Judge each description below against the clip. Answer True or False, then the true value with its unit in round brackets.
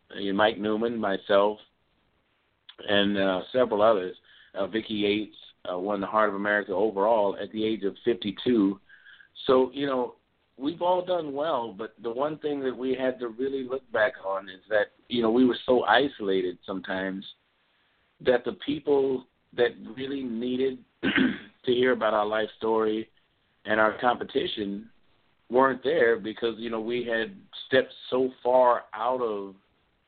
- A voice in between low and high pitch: False (110 Hz)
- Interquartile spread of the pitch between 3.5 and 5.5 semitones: True (4.0 semitones)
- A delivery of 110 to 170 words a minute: True (155 wpm)